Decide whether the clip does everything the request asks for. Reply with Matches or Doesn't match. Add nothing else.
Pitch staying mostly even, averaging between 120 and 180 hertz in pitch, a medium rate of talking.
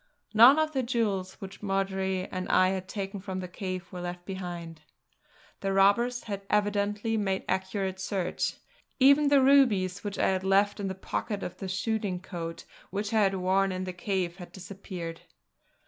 Doesn't match